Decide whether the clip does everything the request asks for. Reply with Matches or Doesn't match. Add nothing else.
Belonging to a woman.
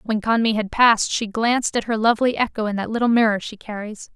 Matches